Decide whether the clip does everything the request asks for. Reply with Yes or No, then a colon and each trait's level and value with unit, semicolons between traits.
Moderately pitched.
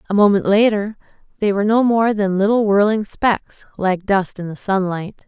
No: high, 205 Hz